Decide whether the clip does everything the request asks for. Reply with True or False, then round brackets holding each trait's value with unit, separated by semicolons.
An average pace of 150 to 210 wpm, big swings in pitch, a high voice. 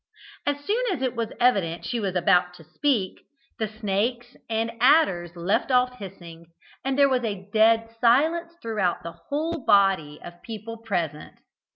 True (160 wpm; 5.8 semitones; 220 Hz)